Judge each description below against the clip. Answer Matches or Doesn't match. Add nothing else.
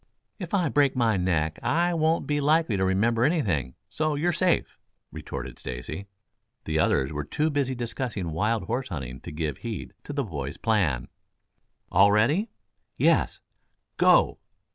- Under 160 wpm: Matches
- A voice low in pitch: Matches